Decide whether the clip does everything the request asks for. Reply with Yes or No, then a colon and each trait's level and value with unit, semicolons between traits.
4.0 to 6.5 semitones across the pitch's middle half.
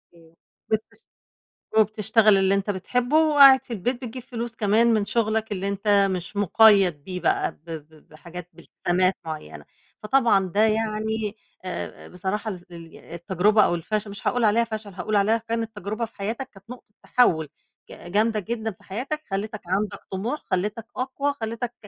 No: average, 3.2 semitones